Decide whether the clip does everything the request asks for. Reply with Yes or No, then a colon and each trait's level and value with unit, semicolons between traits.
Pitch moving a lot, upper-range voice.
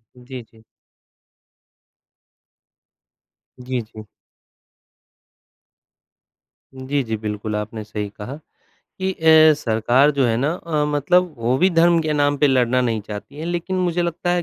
No: wide, 6.1 semitones; low, 135 Hz